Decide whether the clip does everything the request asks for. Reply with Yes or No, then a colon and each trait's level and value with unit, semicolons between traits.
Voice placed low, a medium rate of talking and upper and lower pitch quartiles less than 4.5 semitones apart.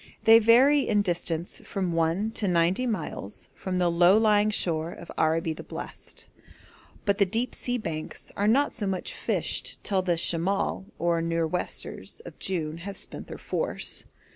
No: medium, 185 Hz; average, 165 wpm; average, 4.1 semitones